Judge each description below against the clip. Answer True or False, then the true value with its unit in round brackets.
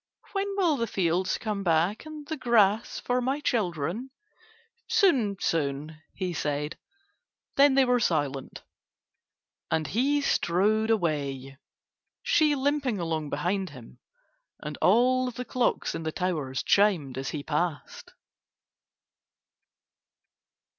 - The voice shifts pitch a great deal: True (8.3 semitones)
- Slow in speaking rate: True (115 wpm)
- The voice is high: True (195 Hz)